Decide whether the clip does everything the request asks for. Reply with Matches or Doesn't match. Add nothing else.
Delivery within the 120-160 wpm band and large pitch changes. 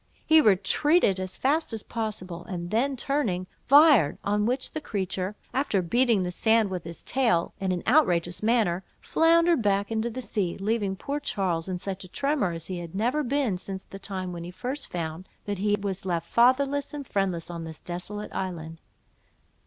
Doesn't match